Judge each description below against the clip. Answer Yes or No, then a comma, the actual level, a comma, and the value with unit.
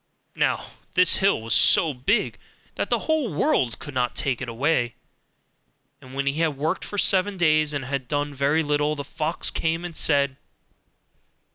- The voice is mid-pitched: Yes, medium, 145 Hz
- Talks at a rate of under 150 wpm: No, average, 170 wpm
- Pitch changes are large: No, average, 3.4 semitones